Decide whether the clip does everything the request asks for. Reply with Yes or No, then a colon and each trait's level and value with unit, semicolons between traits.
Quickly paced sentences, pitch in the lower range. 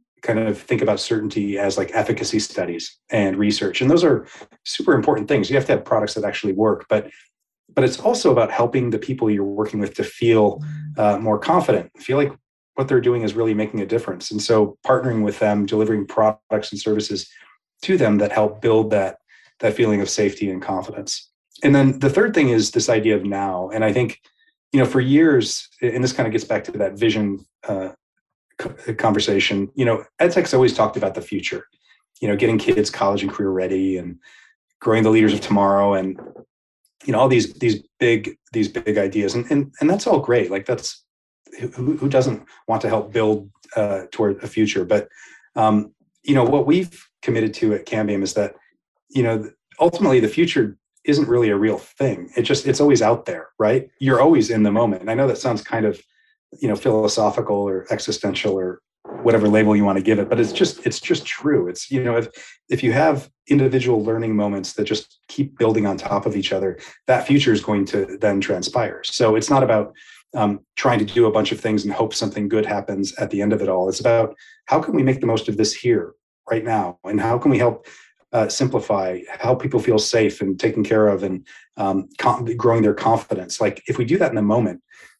Yes: fast, 215 wpm; low, 110 Hz